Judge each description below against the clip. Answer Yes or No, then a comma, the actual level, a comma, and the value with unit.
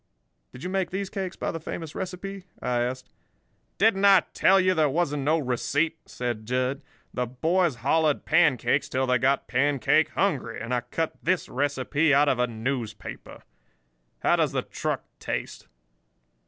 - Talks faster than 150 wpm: Yes, average, 160 wpm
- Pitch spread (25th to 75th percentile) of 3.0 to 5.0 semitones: No, wide, 5.6 semitones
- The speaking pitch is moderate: Yes, medium, 145 Hz